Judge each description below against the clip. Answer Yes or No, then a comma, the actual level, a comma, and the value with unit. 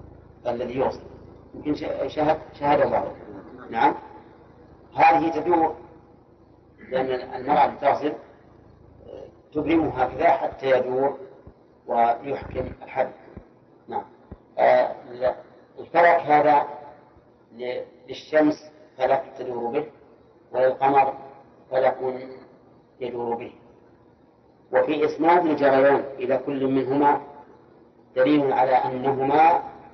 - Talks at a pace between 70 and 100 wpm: Yes, average, 75 wpm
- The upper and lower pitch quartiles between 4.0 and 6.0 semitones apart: No, average, 3.2 semitones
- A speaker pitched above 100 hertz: Yes, low, 135 Hz